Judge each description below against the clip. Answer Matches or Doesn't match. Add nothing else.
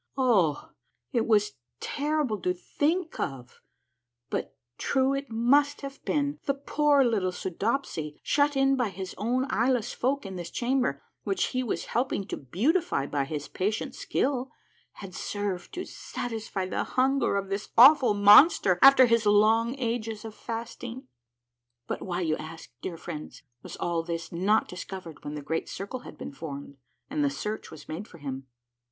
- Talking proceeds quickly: Doesn't match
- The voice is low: Doesn't match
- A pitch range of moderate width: Doesn't match